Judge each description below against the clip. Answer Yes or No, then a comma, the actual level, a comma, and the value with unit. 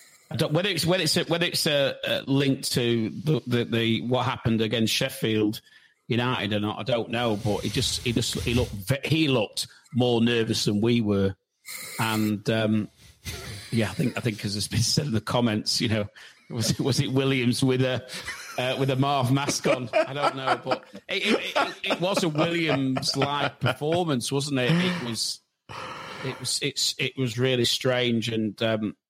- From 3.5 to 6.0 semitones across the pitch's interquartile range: Yes, average, 3.8 semitones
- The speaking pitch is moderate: No, low, 125 Hz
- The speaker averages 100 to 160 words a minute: No, average, 185 wpm